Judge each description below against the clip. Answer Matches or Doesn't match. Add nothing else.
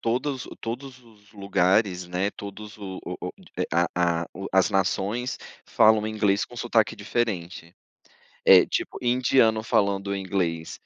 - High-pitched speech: Doesn't match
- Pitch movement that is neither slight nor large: Matches